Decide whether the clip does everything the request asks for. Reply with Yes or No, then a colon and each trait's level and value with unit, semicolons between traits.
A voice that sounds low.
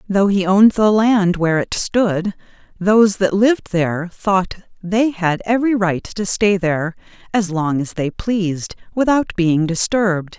No: high, 190 Hz